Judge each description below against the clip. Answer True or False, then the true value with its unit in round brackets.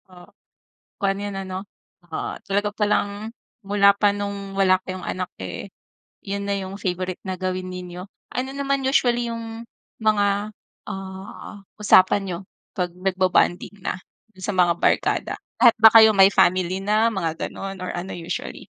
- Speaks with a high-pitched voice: True (195 Hz)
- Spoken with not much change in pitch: True (2.0 semitones)